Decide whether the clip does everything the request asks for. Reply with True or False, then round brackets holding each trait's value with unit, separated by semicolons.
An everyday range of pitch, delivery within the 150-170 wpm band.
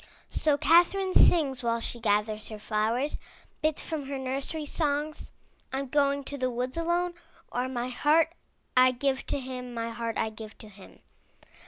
True (4.2 semitones; 165 wpm)